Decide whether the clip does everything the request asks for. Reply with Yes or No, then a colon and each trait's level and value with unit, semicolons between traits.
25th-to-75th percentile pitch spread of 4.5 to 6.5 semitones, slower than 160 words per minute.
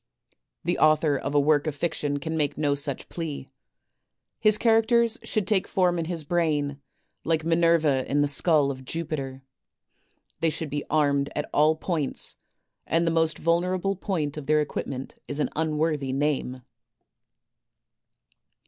No: average, 2.8 semitones; average, 150 wpm